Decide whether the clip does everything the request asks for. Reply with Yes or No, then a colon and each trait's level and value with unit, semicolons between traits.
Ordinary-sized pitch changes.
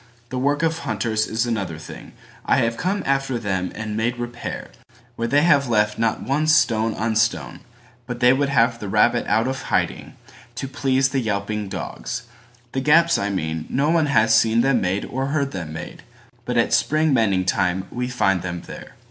Yes: average, 4.3 semitones